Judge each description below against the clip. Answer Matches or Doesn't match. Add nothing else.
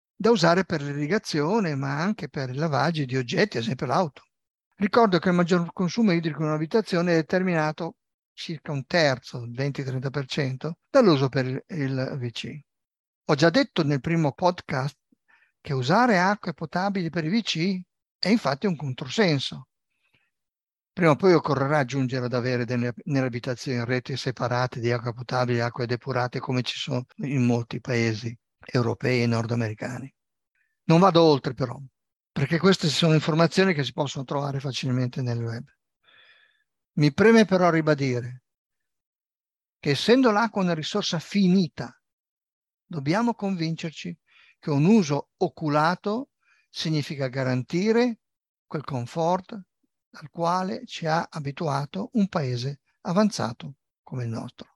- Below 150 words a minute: Matches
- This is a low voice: Doesn't match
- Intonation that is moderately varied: Doesn't match